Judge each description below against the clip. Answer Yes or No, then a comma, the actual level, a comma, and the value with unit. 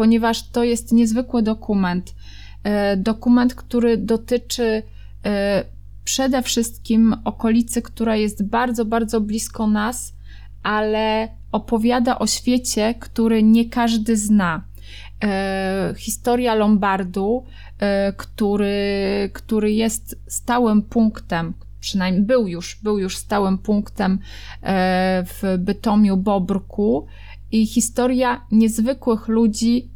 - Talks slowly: Yes, slow, 90 wpm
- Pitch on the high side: Yes, high, 215 Hz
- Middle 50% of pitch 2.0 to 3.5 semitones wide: Yes, average, 3.0 semitones